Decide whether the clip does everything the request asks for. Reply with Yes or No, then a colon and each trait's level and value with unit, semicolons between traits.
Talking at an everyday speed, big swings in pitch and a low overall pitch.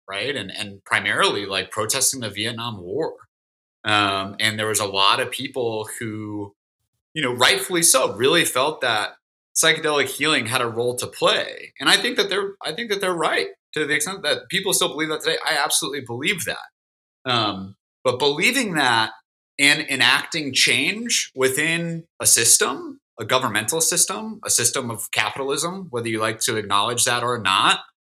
Yes: average, 170 wpm; wide, 7.8 semitones; low, 130 Hz